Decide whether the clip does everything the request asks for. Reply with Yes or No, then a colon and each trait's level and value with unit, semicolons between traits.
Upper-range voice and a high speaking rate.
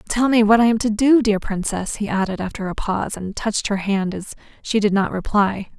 Yes: high, 210 Hz; fast, 240 wpm